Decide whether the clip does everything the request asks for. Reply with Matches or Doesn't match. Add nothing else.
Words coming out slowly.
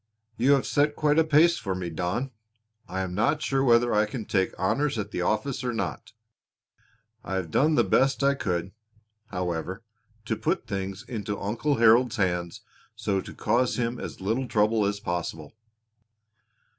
Doesn't match